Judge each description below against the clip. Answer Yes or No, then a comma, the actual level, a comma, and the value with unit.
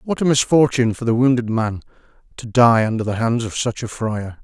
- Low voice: Yes, low, 120 Hz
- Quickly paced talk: Yes, fast, 215 wpm